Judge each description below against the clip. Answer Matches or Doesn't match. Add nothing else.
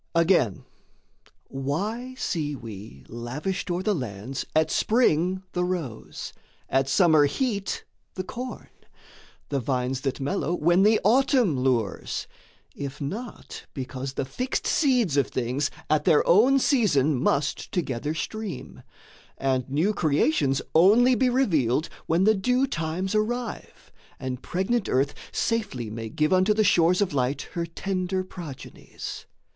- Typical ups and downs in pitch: Doesn't match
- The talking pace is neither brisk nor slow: Doesn't match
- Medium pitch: Matches